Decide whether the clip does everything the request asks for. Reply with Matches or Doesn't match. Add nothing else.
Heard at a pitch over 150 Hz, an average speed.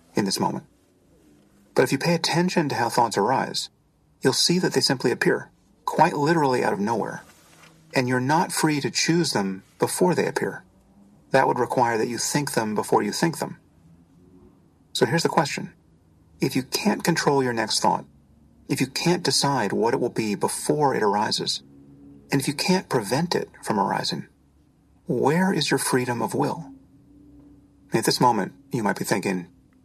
Doesn't match